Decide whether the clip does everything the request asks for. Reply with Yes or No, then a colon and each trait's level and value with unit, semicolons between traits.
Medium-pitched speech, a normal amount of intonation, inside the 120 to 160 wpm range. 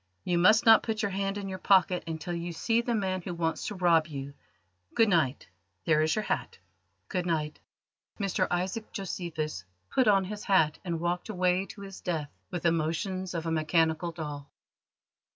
No: medium, 175 Hz; average, 3.3 semitones; average, 185 wpm